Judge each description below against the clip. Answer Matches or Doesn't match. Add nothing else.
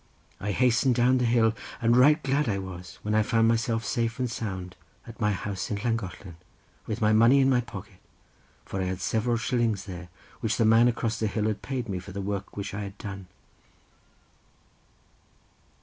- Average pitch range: Matches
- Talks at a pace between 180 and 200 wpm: Matches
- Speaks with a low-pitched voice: Matches